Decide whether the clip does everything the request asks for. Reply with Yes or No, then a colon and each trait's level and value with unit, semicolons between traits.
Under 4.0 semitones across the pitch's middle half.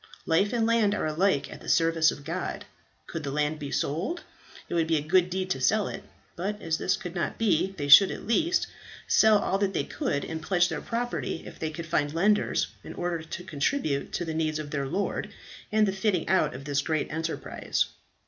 No: average, 4.4 semitones